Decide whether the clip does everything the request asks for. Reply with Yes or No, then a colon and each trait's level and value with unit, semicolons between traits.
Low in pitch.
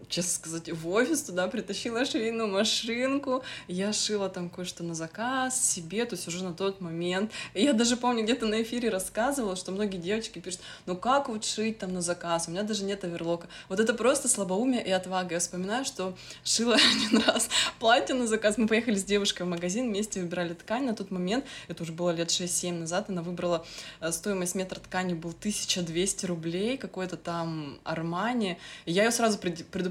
No: high, 190 Hz